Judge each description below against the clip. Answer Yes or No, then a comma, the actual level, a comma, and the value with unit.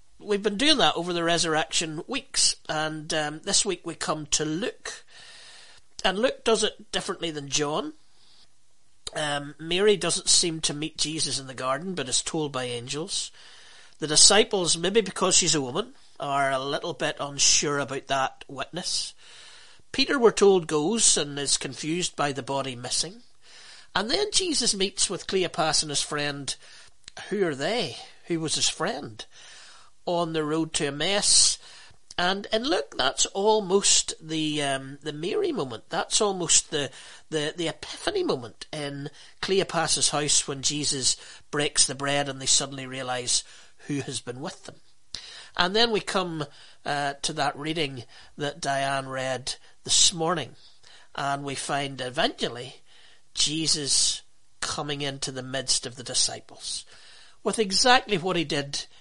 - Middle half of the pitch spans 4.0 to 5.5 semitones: Yes, average, 4.4 semitones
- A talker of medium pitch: Yes, medium, 155 Hz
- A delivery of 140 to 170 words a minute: Yes, average, 155 wpm